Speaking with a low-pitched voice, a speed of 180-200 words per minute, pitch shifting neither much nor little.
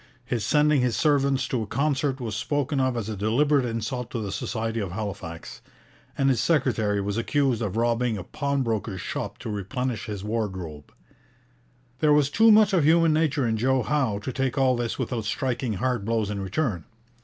Yes: low, 120 Hz; average, 185 wpm; average, 4.5 semitones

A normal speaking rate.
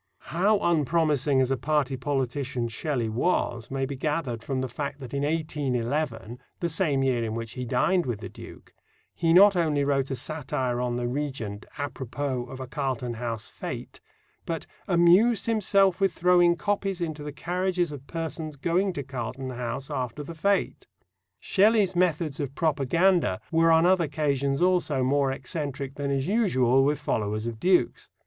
Yes: average, 170 wpm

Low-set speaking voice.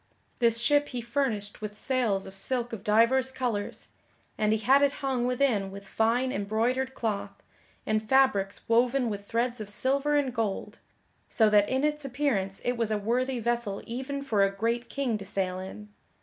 No: high, 235 Hz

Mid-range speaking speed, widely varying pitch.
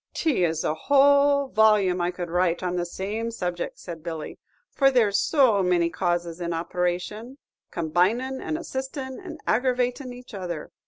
Yes: average, 160 wpm; wide, 6.6 semitones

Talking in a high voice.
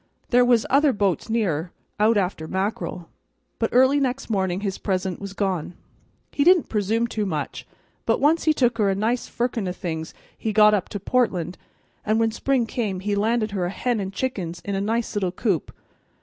Yes: high, 210 Hz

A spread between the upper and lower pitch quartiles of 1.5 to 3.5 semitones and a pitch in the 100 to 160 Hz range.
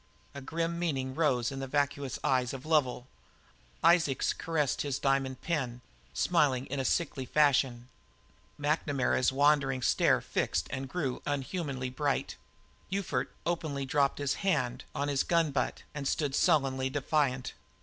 Yes: narrow, 2.5 semitones; medium, 140 Hz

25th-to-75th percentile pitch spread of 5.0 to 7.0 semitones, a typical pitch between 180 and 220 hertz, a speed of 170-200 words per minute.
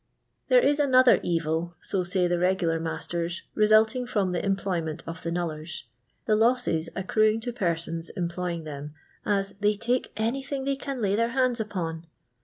Yes: wide, 5.5 semitones; high, 190 Hz; average, 175 wpm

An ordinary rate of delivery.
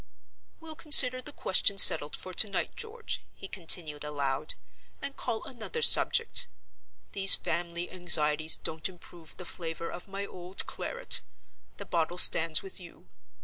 Yes: average, 145 wpm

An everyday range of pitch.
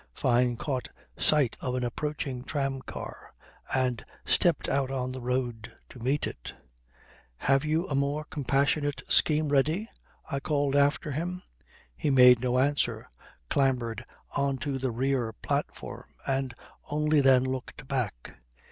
No: narrow, 2.3 semitones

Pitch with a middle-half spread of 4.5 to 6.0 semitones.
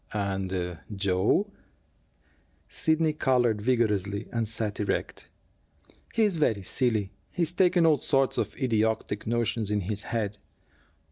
Yes: average, 4.9 semitones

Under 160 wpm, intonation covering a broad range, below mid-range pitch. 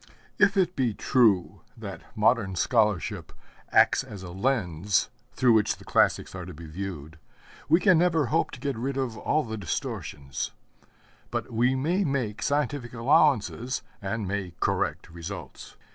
Yes: average, 150 wpm; wide, 6.2 semitones; low, 115 Hz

